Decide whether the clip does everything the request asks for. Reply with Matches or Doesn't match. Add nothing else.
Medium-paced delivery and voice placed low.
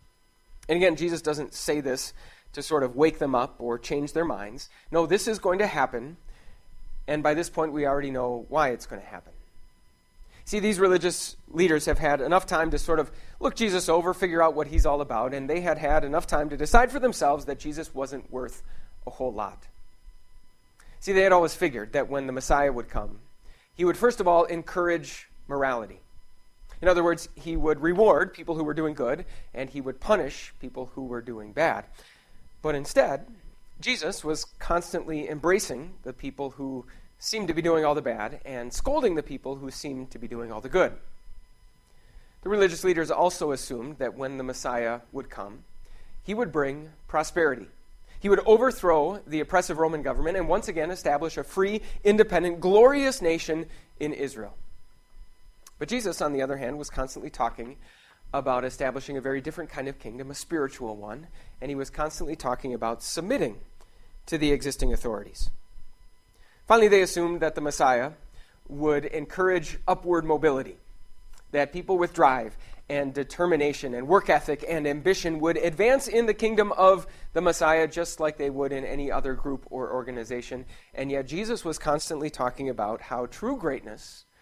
Doesn't match